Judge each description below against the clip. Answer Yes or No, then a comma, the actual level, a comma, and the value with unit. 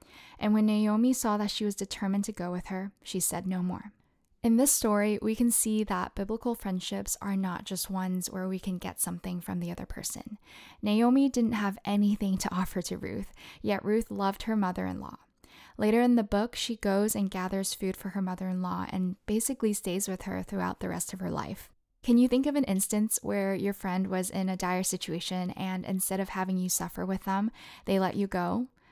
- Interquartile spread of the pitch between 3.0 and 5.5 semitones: No, narrow, 2.6 semitones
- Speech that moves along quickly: Yes, fast, 215 wpm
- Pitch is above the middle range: Yes, high, 195 Hz